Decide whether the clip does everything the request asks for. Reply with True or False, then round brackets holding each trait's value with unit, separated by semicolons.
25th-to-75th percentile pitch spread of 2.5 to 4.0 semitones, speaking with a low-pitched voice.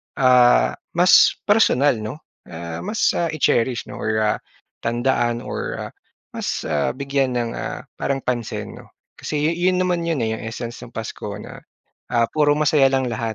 False (4.7 semitones; 130 Hz)